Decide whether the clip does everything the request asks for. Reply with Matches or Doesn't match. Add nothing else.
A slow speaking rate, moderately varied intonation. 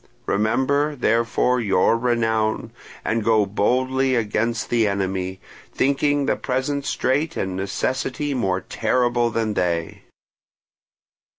Matches